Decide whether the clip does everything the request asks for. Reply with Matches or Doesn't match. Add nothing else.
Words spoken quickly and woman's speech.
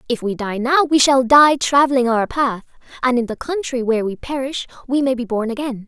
Matches